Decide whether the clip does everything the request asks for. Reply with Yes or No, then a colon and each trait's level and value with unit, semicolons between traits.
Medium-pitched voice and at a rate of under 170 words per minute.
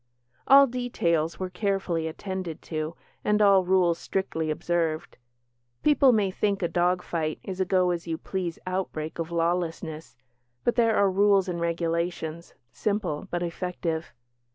Yes: medium, 175 Hz; average, 145 wpm